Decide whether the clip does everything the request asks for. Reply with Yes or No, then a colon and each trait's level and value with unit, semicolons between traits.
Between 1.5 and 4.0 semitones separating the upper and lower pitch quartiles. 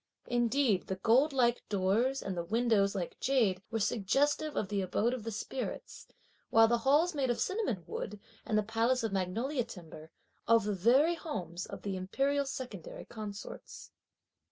No: average, 5.0 semitones